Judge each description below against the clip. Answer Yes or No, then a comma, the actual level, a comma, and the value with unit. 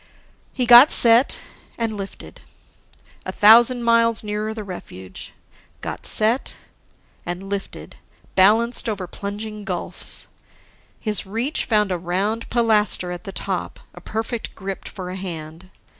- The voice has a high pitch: Yes, high, 210 Hz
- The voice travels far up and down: No, average, 3.4 semitones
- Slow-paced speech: Yes, slow, 130 wpm